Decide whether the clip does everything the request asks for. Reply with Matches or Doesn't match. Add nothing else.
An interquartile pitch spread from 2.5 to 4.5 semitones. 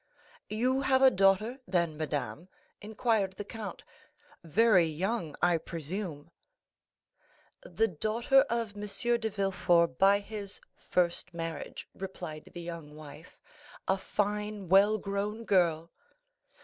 Matches